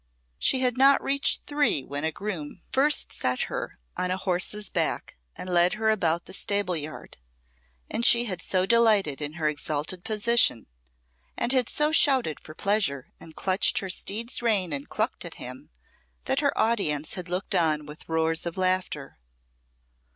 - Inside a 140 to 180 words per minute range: Yes, average, 165 wpm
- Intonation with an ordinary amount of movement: No, wide, 6.3 semitones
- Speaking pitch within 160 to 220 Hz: Yes, medium, 185 Hz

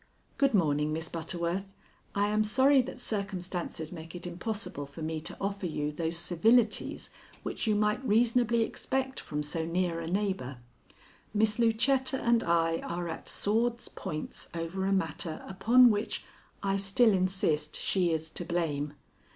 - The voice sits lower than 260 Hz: Yes, high, 190 Hz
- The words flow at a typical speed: Yes, average, 150 wpm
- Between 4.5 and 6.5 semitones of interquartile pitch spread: Yes, average, 5.1 semitones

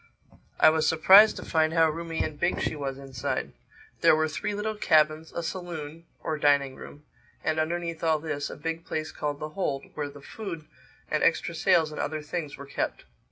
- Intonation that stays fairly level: Yes, narrow, 2.1 semitones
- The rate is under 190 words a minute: No, average, 195 wpm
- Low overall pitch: No, medium, 155 Hz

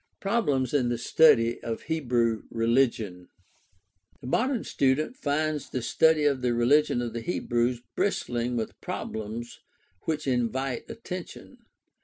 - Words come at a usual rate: No, slow, 130 wpm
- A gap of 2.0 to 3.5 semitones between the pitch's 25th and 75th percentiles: No, average, 4.5 semitones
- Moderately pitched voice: No, low, 125 Hz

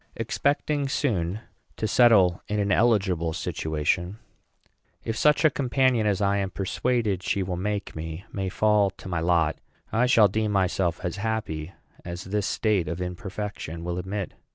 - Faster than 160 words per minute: No, average, 155 wpm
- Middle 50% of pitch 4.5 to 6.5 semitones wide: No, average, 3.8 semitones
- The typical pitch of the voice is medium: No, low, 100 Hz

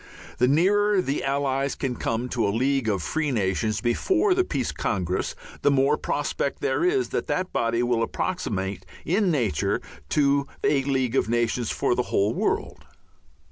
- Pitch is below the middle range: Yes, low, 130 Hz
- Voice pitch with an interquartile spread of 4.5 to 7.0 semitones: Yes, average, 4.8 semitones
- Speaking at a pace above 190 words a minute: No, average, 165 wpm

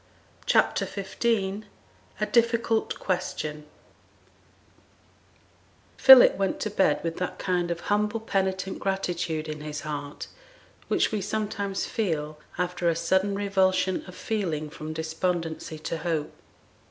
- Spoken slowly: Yes, slow, 115 wpm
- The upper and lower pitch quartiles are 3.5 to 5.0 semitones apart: Yes, average, 4.0 semitones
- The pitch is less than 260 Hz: Yes, medium, 185 Hz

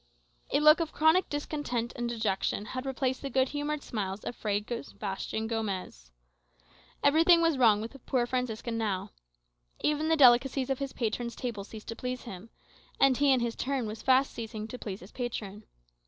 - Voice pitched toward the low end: No, high, 240 Hz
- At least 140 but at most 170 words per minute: No, average, 180 wpm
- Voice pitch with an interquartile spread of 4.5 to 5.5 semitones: No, average, 4.0 semitones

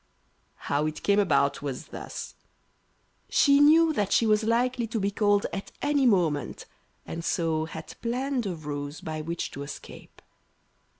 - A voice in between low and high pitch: No, high, 200 Hz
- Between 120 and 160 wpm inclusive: Yes, average, 155 wpm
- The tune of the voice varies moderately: No, wide, 7.3 semitones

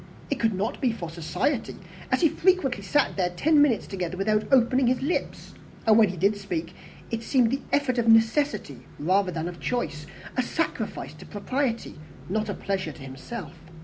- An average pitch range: No, wide, 5.9 semitones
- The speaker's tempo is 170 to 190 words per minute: Yes, average, 180 wpm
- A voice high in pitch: Yes, high, 220 Hz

